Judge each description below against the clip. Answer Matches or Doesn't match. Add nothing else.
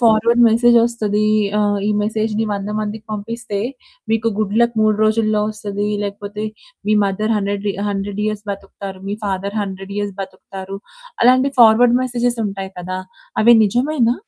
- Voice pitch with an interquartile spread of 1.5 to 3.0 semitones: Matches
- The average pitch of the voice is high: Matches